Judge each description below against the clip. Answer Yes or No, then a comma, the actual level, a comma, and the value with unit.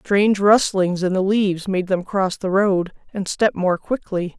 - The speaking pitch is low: No, high, 190 Hz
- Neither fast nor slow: Yes, average, 190 wpm